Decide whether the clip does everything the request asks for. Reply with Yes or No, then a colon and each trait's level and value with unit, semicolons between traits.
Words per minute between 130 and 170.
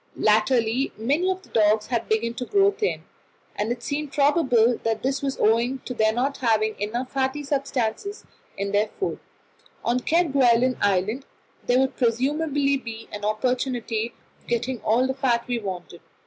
Yes: average, 160 wpm